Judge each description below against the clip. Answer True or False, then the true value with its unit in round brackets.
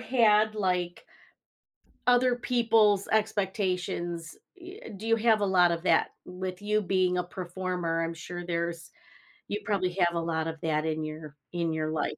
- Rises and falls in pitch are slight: False (3.9 semitones)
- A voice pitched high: False (180 Hz)